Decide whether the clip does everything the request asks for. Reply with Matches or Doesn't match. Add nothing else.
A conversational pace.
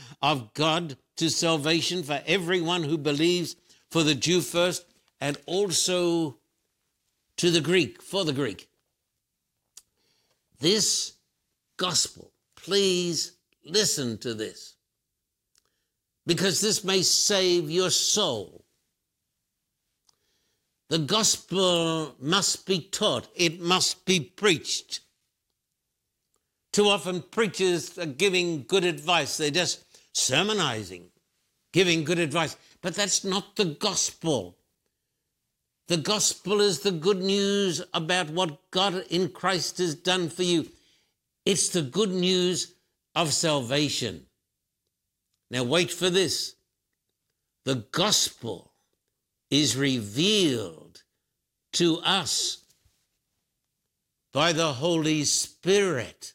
Doesn't match